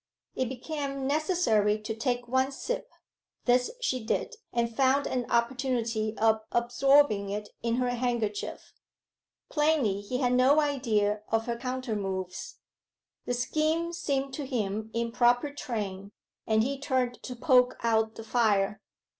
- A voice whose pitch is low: No, high, 245 Hz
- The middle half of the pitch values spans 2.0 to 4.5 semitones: Yes, average, 3.5 semitones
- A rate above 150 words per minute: No, average, 140 wpm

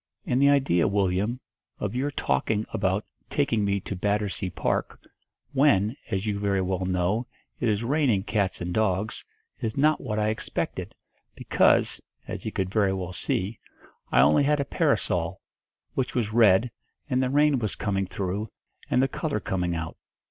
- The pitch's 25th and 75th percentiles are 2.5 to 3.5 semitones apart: No, average, 4.8 semitones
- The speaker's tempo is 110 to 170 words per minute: Yes, average, 165 wpm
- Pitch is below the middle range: Yes, low, 105 Hz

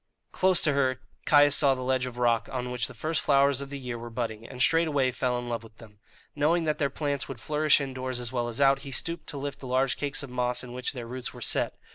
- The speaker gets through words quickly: Yes, fast, 260 wpm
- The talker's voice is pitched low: Yes, low, 130 Hz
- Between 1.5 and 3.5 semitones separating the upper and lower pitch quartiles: Yes, narrow, 2.4 semitones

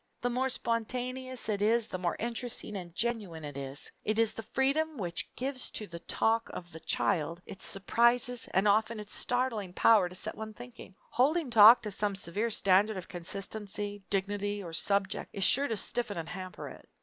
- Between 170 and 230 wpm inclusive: Yes, average, 185 wpm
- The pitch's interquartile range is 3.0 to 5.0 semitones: Yes, average, 3.9 semitones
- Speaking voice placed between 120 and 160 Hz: No, high, 210 Hz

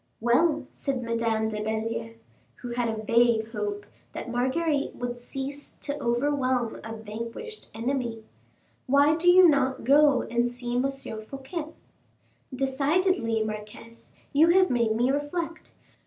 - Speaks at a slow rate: Yes, slow, 130 wpm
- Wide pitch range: No, average, 3.9 semitones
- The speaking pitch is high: Yes, high, 245 Hz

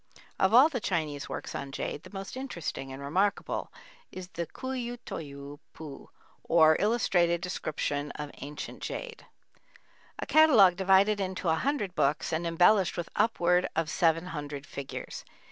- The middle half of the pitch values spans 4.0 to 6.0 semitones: Yes, average, 5.3 semitones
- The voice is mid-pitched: Yes, medium, 175 Hz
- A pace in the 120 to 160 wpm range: Yes, average, 150 wpm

